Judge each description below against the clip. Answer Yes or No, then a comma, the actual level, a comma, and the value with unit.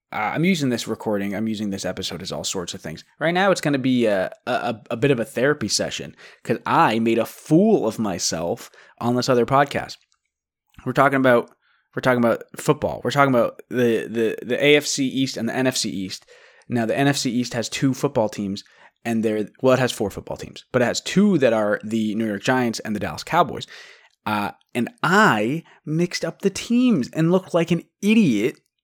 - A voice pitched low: Yes, low, 125 Hz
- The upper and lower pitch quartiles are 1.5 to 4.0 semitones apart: No, average, 4.8 semitones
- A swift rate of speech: Yes, fast, 210 wpm